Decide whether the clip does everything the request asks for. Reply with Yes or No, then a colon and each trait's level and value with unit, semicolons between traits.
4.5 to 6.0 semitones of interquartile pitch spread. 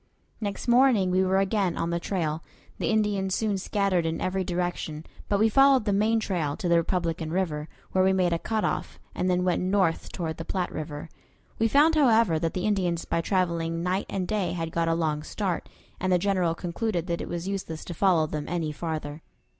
No: average, 3.1 semitones